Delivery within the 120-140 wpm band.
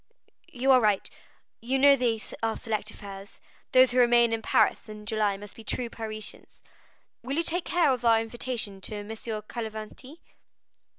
No: average, 165 wpm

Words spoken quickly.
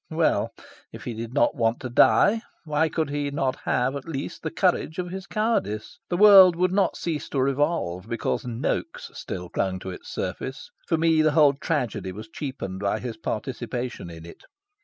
No: average, 185 wpm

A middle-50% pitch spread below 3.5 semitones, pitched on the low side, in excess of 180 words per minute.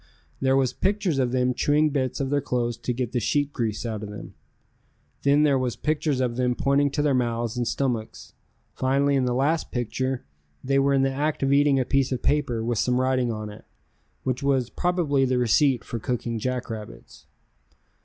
Yes: narrow, 2.5 semitones; low, 130 Hz; average, 195 wpm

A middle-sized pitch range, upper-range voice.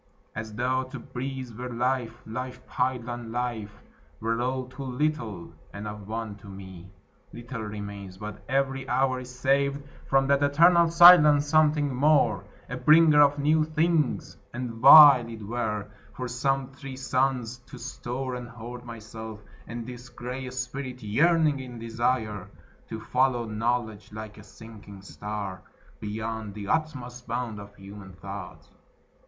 No: average, 3.7 semitones; low, 125 Hz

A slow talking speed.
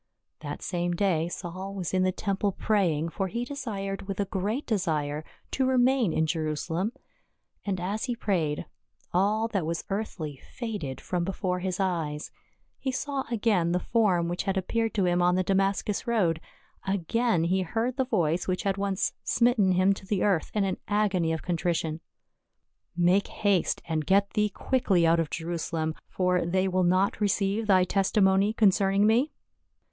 No: average, 175 wpm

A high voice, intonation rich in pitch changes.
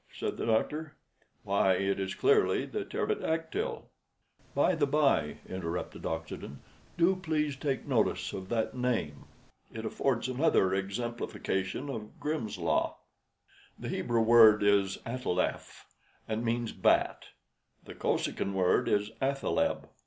No: low, 115 Hz; wide, 7.3 semitones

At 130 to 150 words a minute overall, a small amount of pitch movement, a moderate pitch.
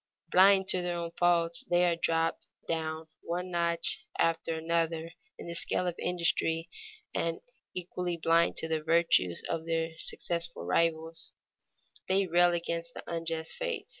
Yes: average, 145 wpm; narrow, 1.1 semitones; medium, 170 Hz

